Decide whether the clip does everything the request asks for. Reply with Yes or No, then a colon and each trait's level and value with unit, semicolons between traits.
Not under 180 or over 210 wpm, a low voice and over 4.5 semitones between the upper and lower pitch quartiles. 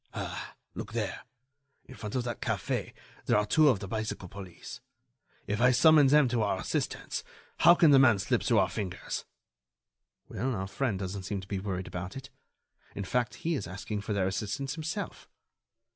Yes: average, 185 wpm; low, 105 Hz; wide, 5.4 semitones